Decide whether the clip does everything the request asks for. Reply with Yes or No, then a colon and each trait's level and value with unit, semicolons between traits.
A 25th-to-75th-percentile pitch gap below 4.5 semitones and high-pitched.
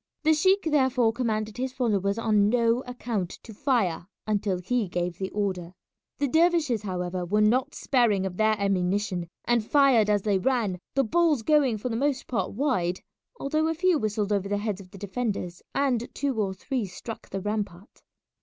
No: average, 4.9 semitones; high, 215 Hz